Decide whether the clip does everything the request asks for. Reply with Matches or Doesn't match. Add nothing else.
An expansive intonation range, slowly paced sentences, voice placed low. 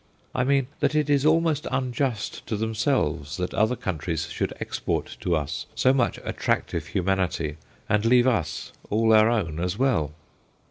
Doesn't match